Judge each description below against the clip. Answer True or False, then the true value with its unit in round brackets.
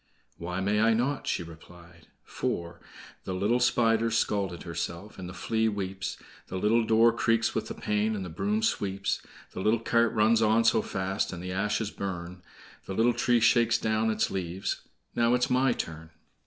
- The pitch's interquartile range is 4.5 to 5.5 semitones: False (3.8 semitones)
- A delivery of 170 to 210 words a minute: True (180 wpm)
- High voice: False (105 Hz)